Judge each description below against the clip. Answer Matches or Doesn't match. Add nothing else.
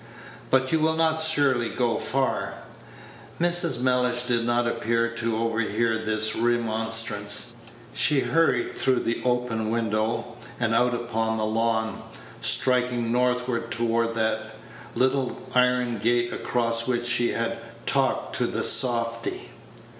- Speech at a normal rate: Doesn't match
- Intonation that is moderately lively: Doesn't match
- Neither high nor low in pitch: Doesn't match